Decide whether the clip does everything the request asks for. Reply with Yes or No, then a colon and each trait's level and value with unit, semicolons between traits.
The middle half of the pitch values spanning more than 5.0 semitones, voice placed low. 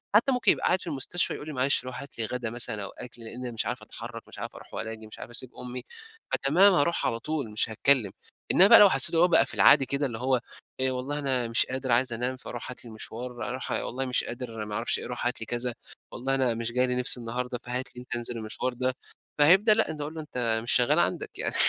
No: average, 2.7 semitones; low, 125 Hz